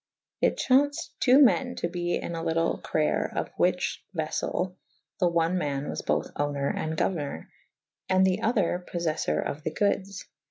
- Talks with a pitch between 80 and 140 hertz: No, medium, 175 Hz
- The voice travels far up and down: No, average, 3.3 semitones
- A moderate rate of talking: Yes, average, 170 wpm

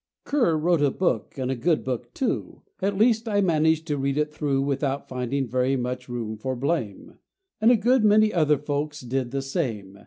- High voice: No, medium, 140 Hz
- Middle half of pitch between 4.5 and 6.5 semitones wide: Yes, average, 5.2 semitones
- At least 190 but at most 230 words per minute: Yes, average, 195 wpm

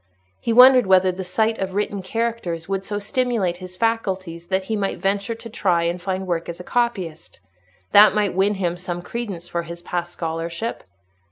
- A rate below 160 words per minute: No, average, 185 wpm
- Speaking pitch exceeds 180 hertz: Yes, high, 190 Hz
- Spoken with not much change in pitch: No, average, 3.5 semitones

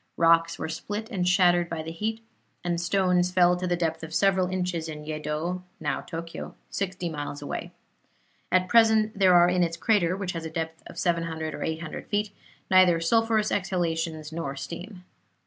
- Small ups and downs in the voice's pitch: Yes, narrow, 2.3 semitones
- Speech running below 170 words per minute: No, average, 175 wpm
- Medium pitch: Yes, medium, 175 Hz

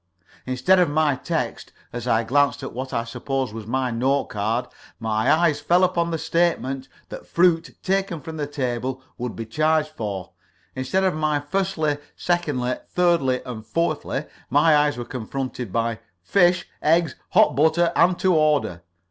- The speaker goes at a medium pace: Yes, average, 160 wpm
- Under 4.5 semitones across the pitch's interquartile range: No, average, 5.1 semitones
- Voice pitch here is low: No, medium, 145 Hz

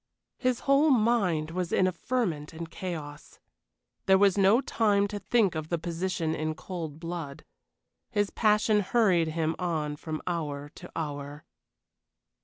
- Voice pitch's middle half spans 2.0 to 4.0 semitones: No, average, 4.6 semitones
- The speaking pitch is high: No, medium, 175 Hz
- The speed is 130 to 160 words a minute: Yes, average, 145 wpm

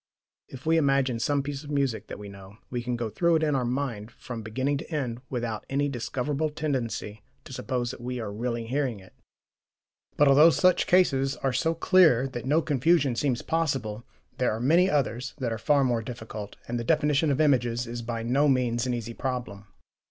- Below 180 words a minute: No, average, 200 wpm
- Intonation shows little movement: No, average, 3.6 semitones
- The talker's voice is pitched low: Yes, low, 130 Hz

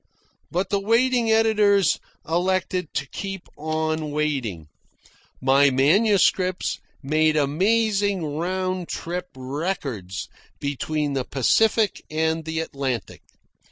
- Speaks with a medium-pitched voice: Yes, medium, 160 Hz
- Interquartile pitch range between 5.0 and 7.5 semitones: Yes, wide, 5.4 semitones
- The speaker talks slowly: Yes, slow, 95 wpm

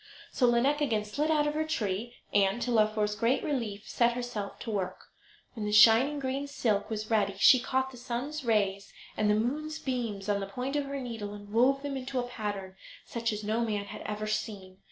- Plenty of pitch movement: No, average, 4.0 semitones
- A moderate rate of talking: No, fast, 210 wpm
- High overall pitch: Yes, high, 230 Hz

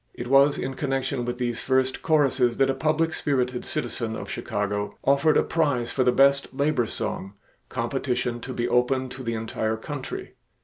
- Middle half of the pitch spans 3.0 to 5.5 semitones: No, narrow, 2.5 semitones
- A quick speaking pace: No, average, 175 wpm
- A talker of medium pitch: No, low, 130 Hz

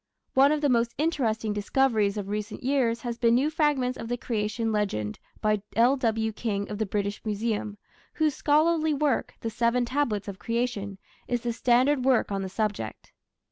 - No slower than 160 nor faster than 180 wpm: Yes, average, 175 wpm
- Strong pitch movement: No, average, 3.9 semitones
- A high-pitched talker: Yes, high, 230 Hz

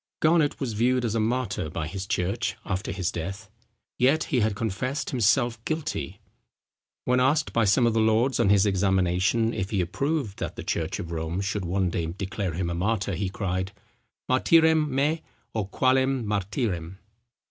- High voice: No, low, 105 Hz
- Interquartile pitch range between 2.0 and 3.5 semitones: No, average, 5.2 semitones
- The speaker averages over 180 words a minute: No, average, 170 wpm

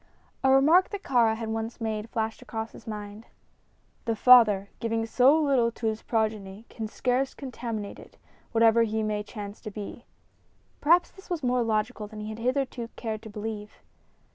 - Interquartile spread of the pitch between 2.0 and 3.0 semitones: Yes, average, 2.7 semitones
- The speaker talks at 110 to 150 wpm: No, average, 170 wpm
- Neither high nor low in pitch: No, high, 225 Hz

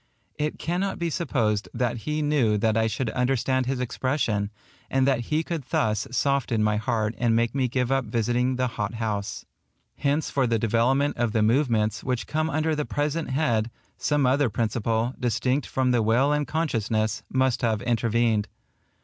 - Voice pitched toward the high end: No, low, 125 Hz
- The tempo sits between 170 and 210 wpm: Yes, average, 175 wpm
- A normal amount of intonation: Yes, average, 3.8 semitones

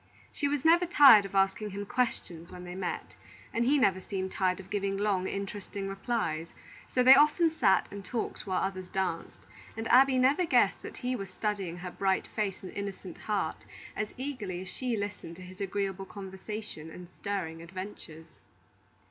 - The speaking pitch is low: No, high, 195 Hz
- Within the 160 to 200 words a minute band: Yes, average, 175 wpm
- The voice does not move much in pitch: No, average, 3.4 semitones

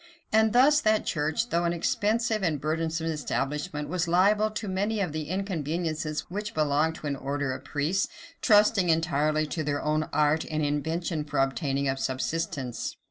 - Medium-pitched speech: Yes, medium, 160 Hz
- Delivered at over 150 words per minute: Yes, average, 165 wpm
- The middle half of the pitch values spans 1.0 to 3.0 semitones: No, average, 4.2 semitones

